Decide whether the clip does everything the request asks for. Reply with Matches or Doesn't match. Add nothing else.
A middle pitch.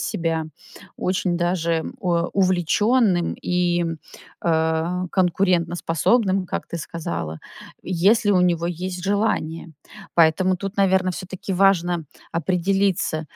Matches